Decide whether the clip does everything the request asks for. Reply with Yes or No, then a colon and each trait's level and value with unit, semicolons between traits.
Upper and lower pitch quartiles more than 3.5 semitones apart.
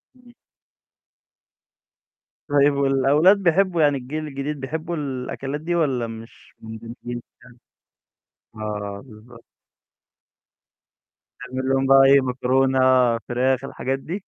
No: average, 2.9 semitones